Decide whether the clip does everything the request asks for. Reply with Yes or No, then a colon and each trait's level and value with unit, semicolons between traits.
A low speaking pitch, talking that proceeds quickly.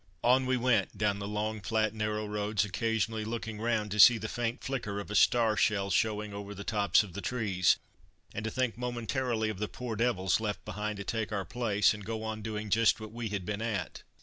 Yes: low, 110 Hz; fast, 220 wpm